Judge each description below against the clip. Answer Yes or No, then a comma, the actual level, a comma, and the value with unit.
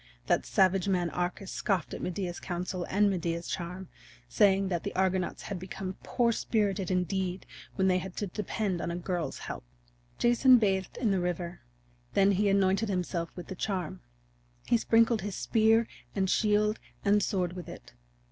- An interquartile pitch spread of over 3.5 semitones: No, narrow, 2.5 semitones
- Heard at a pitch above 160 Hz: Yes, high, 190 Hz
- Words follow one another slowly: No, average, 165 wpm